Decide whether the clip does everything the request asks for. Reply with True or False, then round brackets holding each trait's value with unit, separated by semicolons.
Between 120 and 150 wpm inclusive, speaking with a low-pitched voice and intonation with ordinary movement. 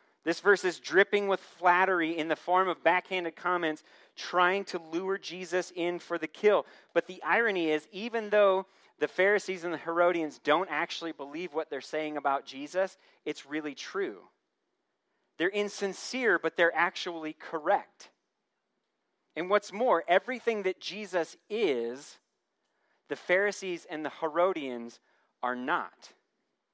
False (140 wpm; 180 Hz; 3.3 semitones)